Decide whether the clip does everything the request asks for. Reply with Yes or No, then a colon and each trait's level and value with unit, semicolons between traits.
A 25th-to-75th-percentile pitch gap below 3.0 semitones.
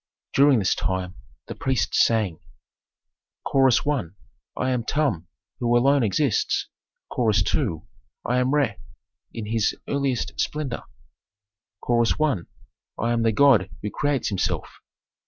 No: average, 4.6 semitones